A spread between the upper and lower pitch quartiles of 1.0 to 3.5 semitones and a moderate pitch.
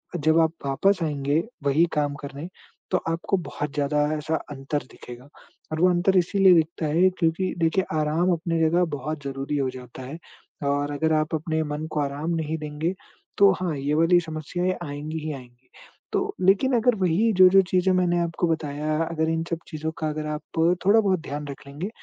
Yes: average, 3.2 semitones; medium, 160 Hz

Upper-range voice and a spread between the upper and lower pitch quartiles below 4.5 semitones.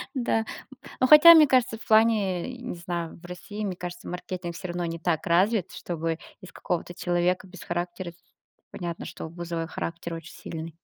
No: medium, 175 Hz; average, 3.6 semitones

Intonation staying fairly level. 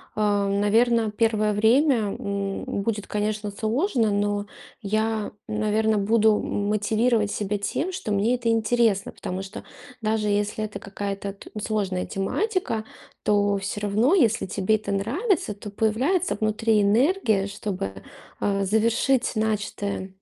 Yes: narrow, 1.9 semitones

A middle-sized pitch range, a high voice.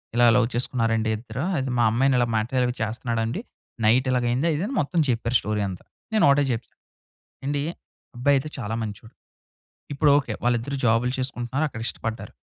No: average, 3.1 semitones; low, 120 Hz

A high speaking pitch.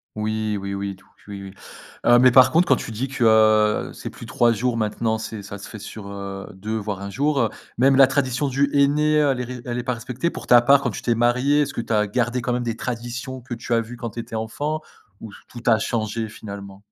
No: low, 115 Hz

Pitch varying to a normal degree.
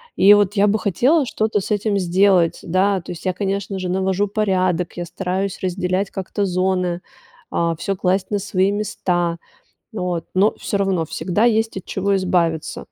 No: narrow, 2.0 semitones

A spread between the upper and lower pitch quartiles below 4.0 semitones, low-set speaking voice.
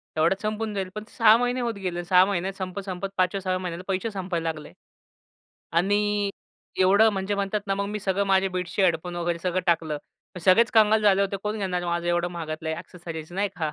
No: average, 2.7 semitones; high, 190 Hz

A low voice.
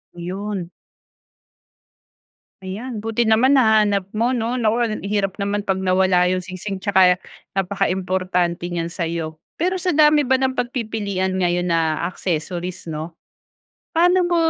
No: high, 195 Hz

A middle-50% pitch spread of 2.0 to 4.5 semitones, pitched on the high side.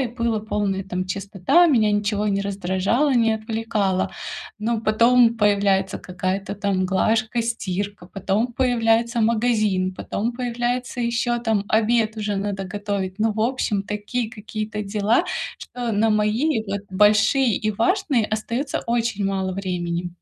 Yes: average, 2.9 semitones; high, 215 Hz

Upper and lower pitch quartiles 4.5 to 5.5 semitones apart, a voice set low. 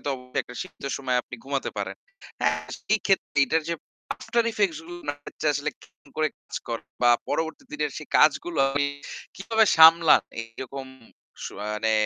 No: average, 5.1 semitones; medium, 150 Hz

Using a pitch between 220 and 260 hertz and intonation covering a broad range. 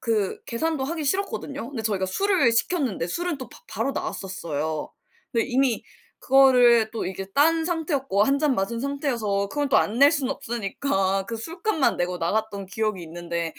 Yes: high, 235 Hz; wide, 6.3 semitones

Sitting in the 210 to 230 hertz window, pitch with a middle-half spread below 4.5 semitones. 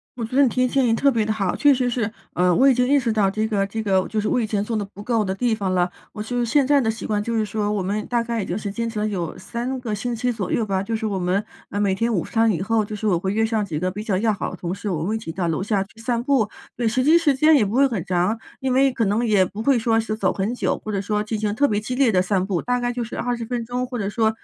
Yes: high, 220 Hz; average, 3.3 semitones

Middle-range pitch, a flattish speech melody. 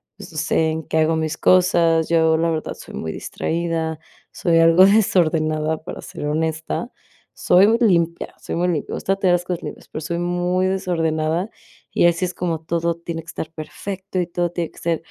Yes: medium, 170 Hz; narrow, 1.8 semitones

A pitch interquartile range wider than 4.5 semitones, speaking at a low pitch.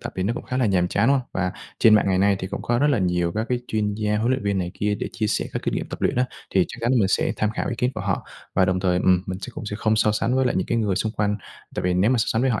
No: average, 3.8 semitones; low, 105 Hz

